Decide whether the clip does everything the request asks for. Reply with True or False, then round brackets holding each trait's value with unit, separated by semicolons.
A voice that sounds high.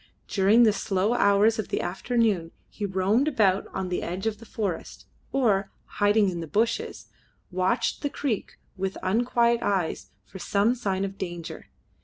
True (200 Hz)